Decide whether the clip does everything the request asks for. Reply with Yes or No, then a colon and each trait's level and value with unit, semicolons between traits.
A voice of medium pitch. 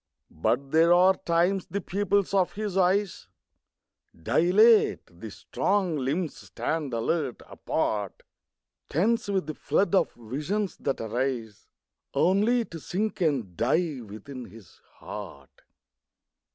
Yes: medium, 165 Hz